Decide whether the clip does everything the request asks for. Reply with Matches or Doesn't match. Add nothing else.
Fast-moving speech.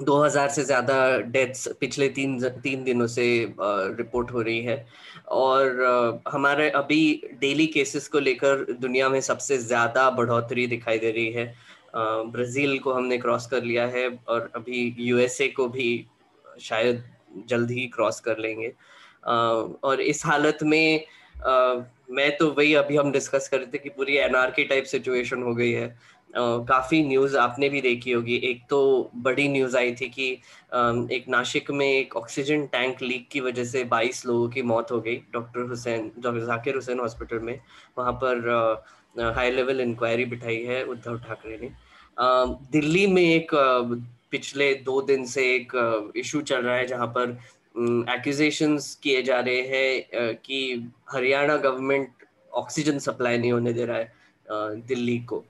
Doesn't match